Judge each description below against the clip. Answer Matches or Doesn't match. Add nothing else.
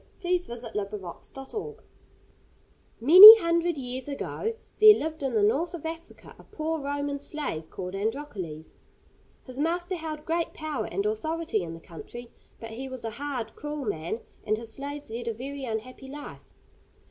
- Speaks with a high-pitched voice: Matches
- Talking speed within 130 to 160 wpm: Doesn't match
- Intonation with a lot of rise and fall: Matches